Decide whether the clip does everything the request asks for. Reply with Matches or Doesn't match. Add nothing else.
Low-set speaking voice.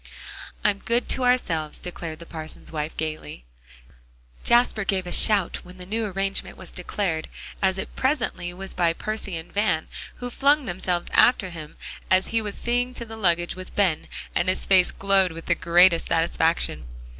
Doesn't match